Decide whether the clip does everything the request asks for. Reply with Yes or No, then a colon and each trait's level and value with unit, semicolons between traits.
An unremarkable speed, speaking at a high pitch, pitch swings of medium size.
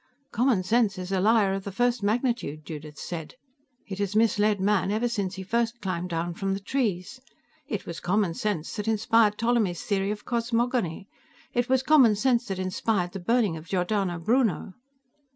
Yes: average, 175 wpm; high, 205 Hz; average, 4.1 semitones